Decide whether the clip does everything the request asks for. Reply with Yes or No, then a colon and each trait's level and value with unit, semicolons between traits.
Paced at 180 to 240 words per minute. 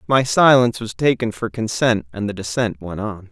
Yes: average, 200 wpm